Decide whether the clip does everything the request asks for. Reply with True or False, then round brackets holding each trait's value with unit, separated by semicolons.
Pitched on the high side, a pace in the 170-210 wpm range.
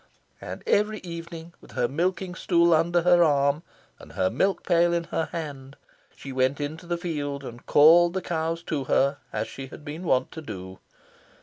False (160 Hz; 185 wpm)